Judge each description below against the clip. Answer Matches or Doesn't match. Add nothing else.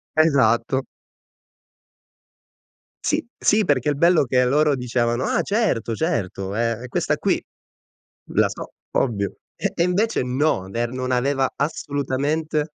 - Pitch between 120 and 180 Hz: Matches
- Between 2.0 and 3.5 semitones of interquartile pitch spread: Doesn't match